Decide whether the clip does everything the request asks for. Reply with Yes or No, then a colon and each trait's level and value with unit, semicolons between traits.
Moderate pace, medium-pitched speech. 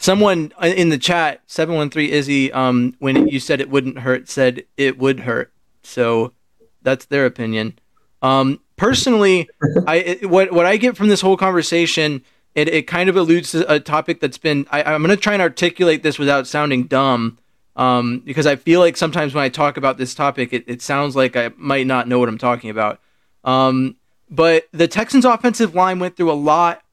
Yes: average, 195 wpm; medium, 145 Hz